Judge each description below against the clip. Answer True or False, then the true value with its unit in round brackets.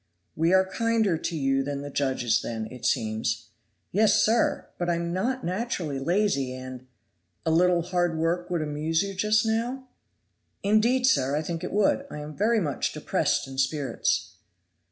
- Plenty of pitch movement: True (7.2 semitones)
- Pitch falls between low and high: True (170 Hz)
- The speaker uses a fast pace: False (175 wpm)